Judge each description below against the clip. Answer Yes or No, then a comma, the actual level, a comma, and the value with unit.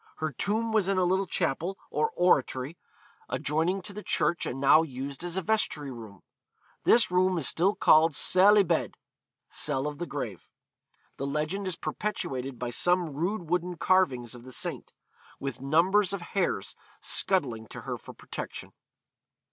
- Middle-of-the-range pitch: Yes, medium, 165 Hz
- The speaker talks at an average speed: Yes, average, 165 wpm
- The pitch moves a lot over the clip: Yes, wide, 5.7 semitones